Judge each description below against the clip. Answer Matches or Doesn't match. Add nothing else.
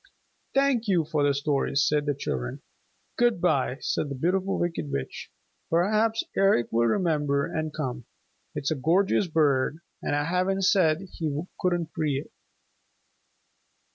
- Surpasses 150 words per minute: Doesn't match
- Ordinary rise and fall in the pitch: Matches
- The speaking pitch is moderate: Matches